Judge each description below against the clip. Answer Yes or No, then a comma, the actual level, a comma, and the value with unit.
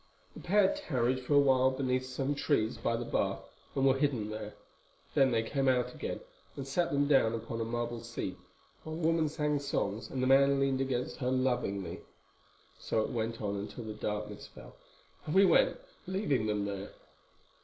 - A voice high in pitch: No, low, 130 Hz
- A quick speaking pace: No, average, 185 wpm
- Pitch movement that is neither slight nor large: Yes, average, 3.8 semitones